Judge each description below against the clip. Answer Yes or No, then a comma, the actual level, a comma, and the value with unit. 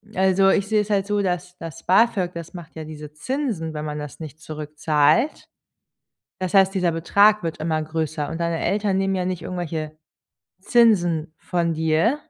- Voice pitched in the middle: Yes, medium, 170 Hz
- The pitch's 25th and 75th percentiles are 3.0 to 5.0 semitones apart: Yes, average, 3.6 semitones